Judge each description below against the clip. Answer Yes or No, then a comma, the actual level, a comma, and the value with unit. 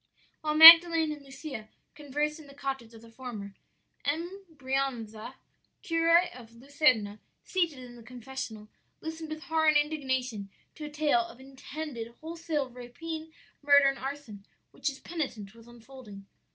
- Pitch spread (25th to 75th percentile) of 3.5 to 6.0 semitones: Yes, average, 4.7 semitones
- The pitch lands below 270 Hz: No, very high, 275 Hz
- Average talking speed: Yes, average, 145 wpm